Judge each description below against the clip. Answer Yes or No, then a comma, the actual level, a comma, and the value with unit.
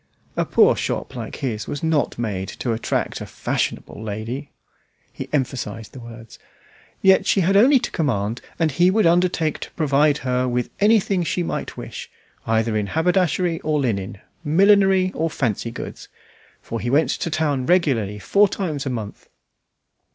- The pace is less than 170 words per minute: Yes, average, 160 wpm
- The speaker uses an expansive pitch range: Yes, wide, 7.4 semitones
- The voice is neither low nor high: Yes, medium, 145 Hz